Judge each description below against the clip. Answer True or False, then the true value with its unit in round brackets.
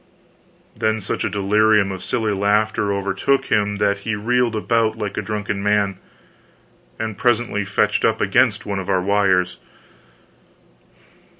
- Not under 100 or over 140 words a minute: True (135 wpm)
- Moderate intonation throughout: False (1.6 semitones)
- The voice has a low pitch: True (105 Hz)